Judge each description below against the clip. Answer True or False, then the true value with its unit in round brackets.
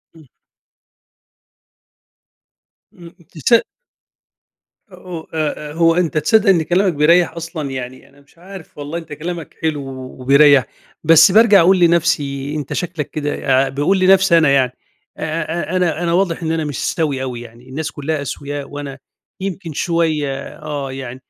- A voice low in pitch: False (155 Hz)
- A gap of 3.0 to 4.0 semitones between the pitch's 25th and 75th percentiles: True (3.3 semitones)